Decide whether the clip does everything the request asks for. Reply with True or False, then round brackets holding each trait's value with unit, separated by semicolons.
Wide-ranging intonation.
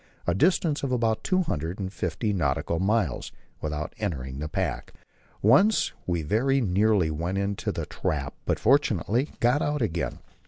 True (7.3 semitones)